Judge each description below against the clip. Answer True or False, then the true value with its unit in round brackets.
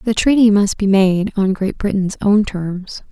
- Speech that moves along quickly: False (195 wpm)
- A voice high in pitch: True (200 Hz)